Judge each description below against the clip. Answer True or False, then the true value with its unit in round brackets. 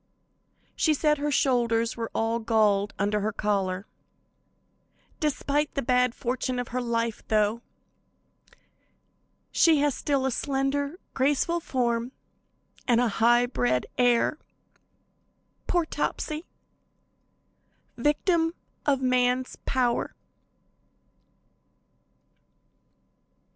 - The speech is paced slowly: True (90 wpm)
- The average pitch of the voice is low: False (250 Hz)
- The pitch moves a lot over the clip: False (3.7 semitones)